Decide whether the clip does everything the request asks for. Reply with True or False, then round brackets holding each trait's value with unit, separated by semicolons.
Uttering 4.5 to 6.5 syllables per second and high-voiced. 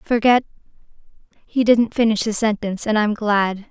True (4.9 syllables/s; 220 Hz)